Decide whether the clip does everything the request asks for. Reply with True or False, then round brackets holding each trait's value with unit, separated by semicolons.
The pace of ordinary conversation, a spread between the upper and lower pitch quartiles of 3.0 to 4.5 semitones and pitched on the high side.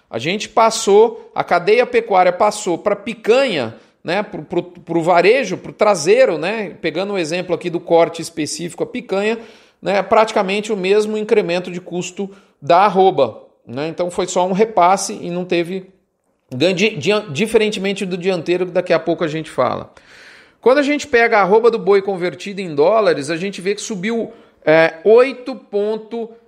True (170 wpm; 3.9 semitones; 200 Hz)